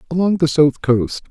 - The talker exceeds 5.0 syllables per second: No, 4.8 syllables/s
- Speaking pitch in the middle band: Yes, medium, 155 Hz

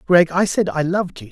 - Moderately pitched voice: Yes, medium, 175 Hz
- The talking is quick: Yes, fast, 275 wpm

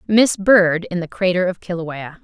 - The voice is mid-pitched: Yes, medium, 180 Hz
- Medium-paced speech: Yes, average, 190 wpm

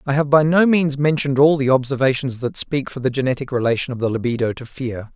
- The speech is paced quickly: Yes, fast, 235 wpm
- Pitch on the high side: No, low, 135 Hz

